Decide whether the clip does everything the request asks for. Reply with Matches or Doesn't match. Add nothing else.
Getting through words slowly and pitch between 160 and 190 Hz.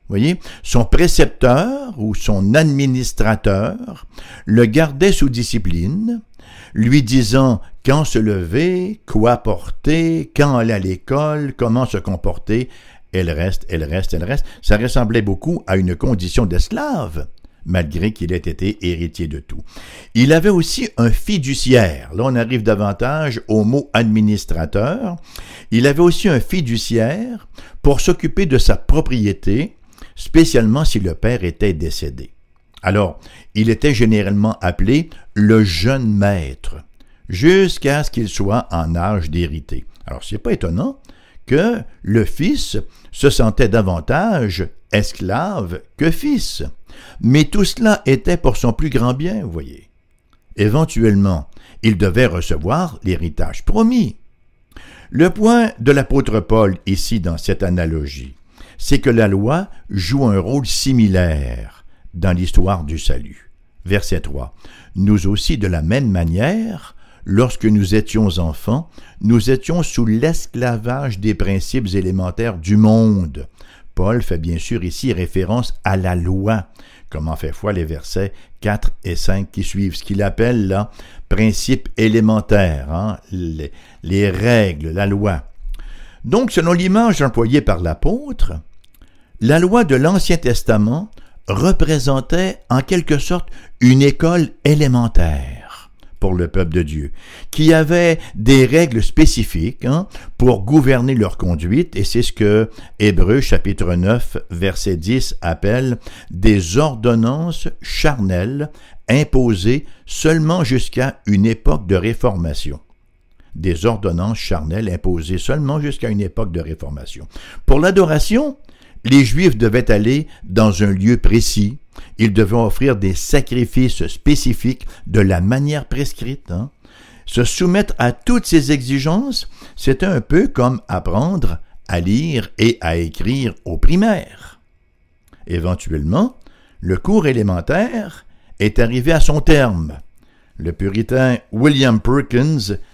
Doesn't match